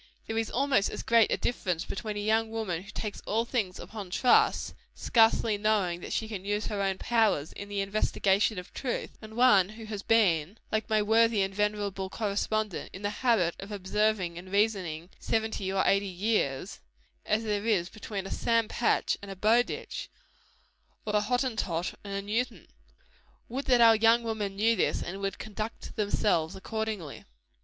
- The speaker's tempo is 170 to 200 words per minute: Yes, average, 175 wpm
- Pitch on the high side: Yes, high, 210 Hz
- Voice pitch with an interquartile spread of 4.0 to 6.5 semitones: No, narrow, 2.4 semitones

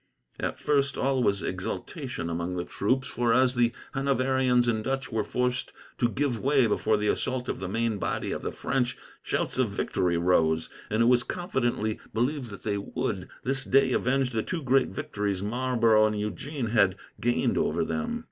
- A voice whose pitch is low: Yes, low, 120 Hz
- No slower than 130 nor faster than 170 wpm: No, average, 180 wpm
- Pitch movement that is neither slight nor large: Yes, average, 3.9 semitones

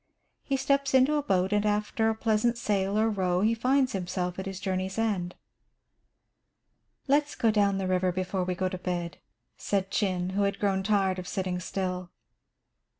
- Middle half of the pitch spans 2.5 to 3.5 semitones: Yes, average, 3.1 semitones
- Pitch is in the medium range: No, high, 195 Hz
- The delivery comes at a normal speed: Yes, average, 175 wpm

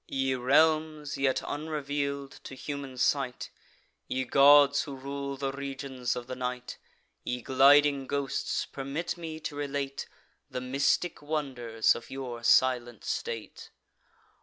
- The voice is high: No, medium, 140 Hz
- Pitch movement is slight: Yes, narrow, 1.9 semitones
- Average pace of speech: No, slow, 125 wpm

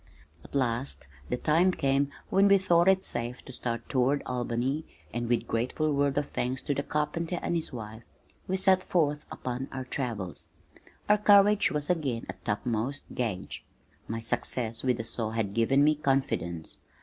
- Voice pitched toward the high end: No, low, 135 Hz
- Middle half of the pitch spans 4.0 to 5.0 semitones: Yes, average, 4.7 semitones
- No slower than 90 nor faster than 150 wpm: No, average, 170 wpm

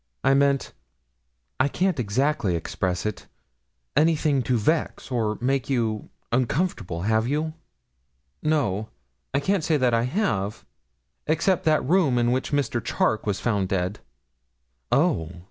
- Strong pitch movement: Yes, wide, 6.0 semitones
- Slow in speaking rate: Yes, slow, 130 wpm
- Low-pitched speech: Yes, low, 130 Hz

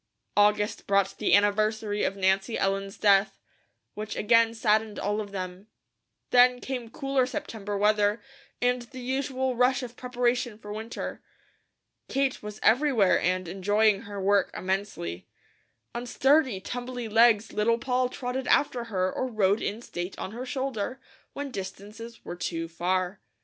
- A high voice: Yes, high, 215 Hz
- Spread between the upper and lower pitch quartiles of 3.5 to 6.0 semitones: Yes, average, 3.8 semitones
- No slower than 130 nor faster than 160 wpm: Yes, average, 145 wpm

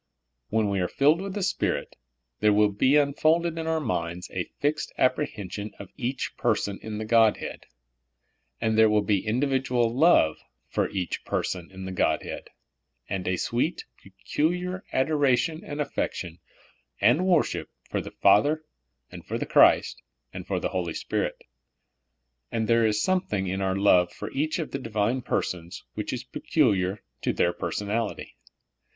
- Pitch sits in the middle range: No, low, 115 Hz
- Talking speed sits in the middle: Yes, average, 160 wpm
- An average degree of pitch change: No, wide, 6.9 semitones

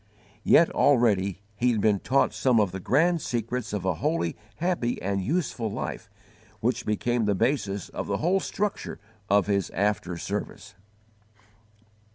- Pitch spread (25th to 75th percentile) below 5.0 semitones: No, wide, 5.5 semitones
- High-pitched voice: No, low, 110 Hz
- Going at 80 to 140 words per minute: No, average, 150 wpm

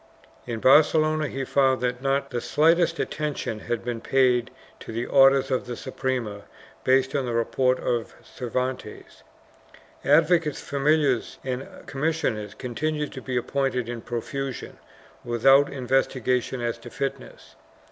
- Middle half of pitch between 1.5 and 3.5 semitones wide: Yes, narrow, 2.6 semitones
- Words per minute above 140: No, slow, 135 wpm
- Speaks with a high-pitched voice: No, low, 130 Hz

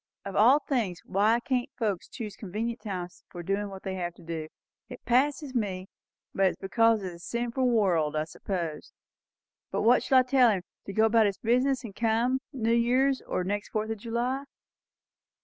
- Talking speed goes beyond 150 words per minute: Yes, average, 185 wpm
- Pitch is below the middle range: No, high, 220 Hz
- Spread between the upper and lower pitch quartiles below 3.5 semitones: No, average, 4.2 semitones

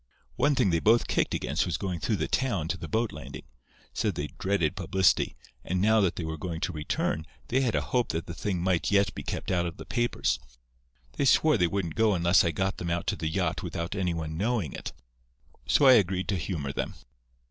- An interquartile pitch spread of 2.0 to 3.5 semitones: No, average, 4.0 semitones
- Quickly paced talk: Yes, fast, 225 wpm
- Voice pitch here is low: Yes, very low, 90 Hz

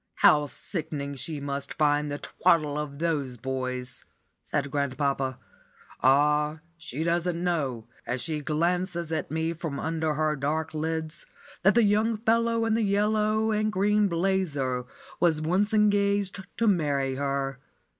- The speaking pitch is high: No, medium, 160 Hz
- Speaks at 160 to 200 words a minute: No, average, 140 wpm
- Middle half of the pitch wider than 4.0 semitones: Yes, average, 5.3 semitones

